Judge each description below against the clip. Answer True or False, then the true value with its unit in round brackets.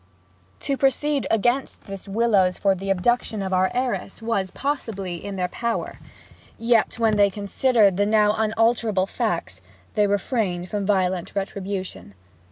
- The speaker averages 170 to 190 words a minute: False (140 wpm)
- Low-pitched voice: False (205 Hz)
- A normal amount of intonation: True (3.4 semitones)